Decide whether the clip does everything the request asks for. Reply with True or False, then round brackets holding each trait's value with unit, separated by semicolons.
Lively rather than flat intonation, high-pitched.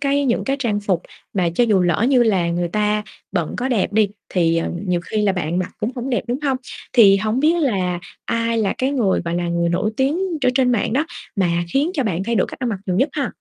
True (5.8 semitones; 210 Hz)